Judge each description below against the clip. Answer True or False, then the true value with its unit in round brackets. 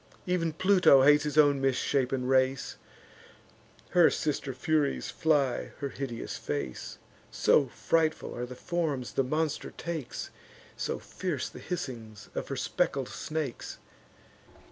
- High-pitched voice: False (140 Hz)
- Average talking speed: False (120 wpm)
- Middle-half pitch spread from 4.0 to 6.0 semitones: False (3.4 semitones)